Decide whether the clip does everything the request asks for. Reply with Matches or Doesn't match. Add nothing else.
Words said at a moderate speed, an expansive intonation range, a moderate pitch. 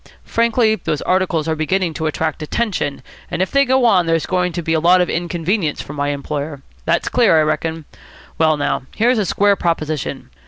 Doesn't match